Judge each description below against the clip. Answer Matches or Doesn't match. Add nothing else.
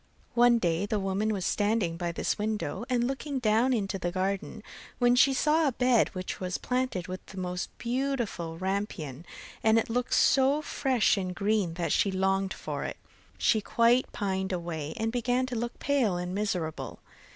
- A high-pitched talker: Matches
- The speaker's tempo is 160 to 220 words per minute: Matches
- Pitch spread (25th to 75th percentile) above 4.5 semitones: Matches